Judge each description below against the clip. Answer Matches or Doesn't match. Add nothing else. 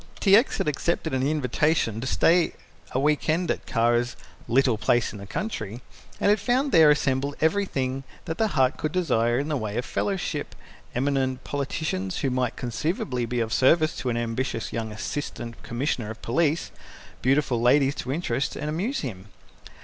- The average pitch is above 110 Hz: Matches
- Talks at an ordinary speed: Matches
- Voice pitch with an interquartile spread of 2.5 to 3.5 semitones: Doesn't match